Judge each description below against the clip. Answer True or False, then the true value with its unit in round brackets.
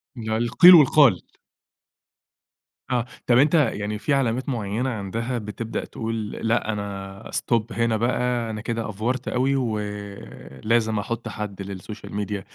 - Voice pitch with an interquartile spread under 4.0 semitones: True (2.9 semitones)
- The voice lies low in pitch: True (115 Hz)